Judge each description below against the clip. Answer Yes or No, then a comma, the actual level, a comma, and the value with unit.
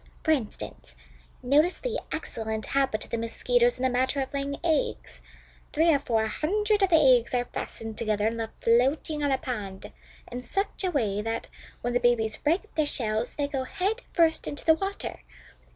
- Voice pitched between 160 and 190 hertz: No, very high, 270 Hz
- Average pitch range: No, wide, 5.8 semitones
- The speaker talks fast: No, average, 185 wpm